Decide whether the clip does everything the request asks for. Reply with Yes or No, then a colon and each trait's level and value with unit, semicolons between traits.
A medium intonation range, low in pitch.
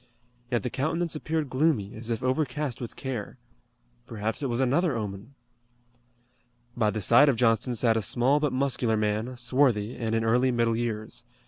Yes: average, 3.2 semitones; low, 120 Hz